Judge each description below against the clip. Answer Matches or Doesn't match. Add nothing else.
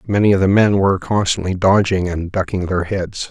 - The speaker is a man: Matches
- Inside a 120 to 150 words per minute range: Doesn't match